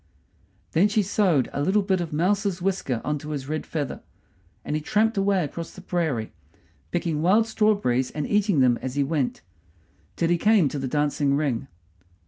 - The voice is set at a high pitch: No, medium, 165 Hz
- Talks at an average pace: Yes, average, 185 wpm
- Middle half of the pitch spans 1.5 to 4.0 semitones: No, wide, 5.6 semitones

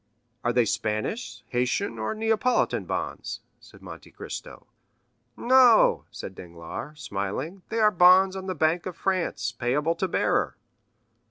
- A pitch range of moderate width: No, wide, 8.2 semitones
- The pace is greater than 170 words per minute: No, slow, 135 wpm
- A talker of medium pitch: Yes, medium, 170 Hz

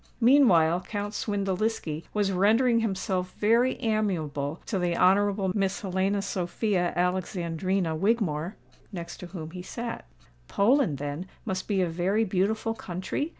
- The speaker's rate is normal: No, slow, 130 wpm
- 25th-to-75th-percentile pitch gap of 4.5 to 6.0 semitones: No, average, 3.4 semitones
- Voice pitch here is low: No, high, 190 Hz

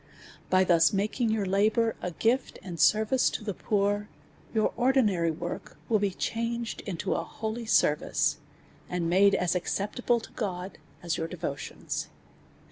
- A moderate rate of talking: Yes, average, 145 wpm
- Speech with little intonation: No, average, 3.9 semitones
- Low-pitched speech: No, high, 200 Hz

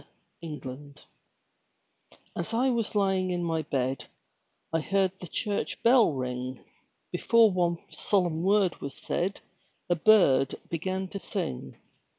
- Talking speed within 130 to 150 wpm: Yes, slow, 135 wpm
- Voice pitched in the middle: Yes, medium, 175 Hz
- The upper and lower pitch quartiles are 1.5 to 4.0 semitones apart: No, average, 5.3 semitones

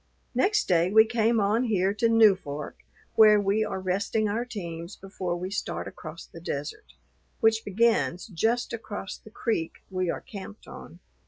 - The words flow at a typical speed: Yes, average, 160 wpm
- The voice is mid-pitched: No, high, 205 Hz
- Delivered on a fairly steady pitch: No, average, 3.7 semitones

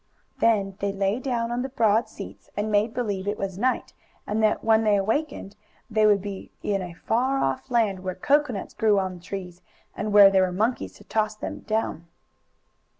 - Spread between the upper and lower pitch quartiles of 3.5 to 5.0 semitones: No, average, 2.7 semitones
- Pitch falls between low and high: No, high, 210 Hz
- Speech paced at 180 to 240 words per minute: Yes, average, 190 wpm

